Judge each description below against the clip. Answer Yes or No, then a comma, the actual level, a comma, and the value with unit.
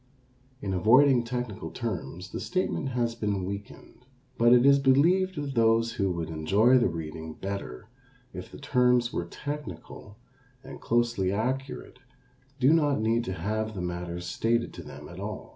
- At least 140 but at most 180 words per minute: Yes, average, 160 wpm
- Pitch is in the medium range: No, low, 115 Hz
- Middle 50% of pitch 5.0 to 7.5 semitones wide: Yes, average, 5.3 semitones